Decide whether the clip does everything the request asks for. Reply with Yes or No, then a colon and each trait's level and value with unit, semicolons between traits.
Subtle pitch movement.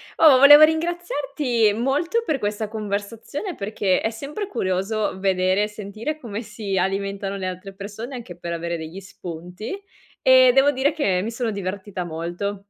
No: wide, 5.8 semitones